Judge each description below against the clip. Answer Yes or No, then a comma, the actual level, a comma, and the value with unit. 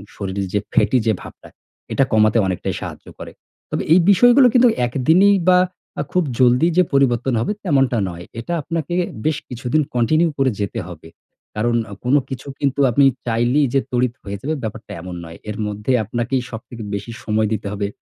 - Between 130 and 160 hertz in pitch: No, low, 120 Hz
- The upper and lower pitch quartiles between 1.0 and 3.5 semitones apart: No, wide, 5.4 semitones